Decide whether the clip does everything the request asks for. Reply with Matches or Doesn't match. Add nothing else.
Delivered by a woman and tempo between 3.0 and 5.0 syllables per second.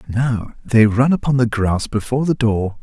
Doesn't match